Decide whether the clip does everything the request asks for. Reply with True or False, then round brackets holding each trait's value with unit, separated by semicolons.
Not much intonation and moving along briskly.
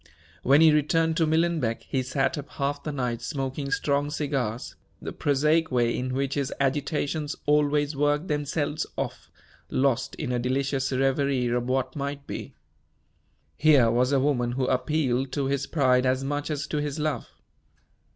False (2.3 semitones; 160 wpm)